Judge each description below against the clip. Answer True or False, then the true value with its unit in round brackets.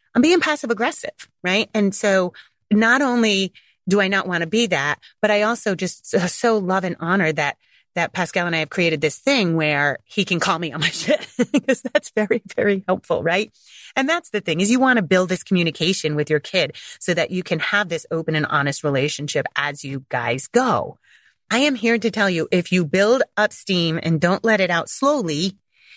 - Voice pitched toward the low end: False (190 Hz)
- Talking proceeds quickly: True (215 wpm)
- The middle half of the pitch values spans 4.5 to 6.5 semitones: True (5.5 semitones)